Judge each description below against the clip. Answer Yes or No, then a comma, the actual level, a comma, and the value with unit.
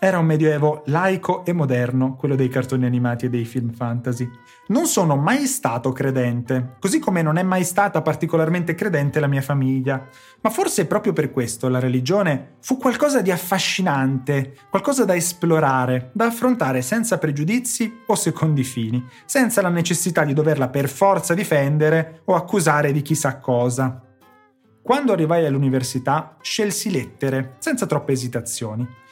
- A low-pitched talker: No, medium, 150 Hz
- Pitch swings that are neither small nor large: No, wide, 6.5 semitones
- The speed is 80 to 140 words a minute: No, average, 150 wpm